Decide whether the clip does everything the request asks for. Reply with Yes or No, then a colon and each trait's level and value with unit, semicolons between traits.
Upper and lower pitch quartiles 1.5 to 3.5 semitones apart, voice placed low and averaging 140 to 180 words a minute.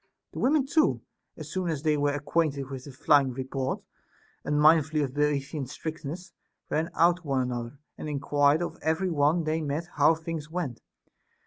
No: average, 2.8 semitones; medium, 150 Hz; average, 175 wpm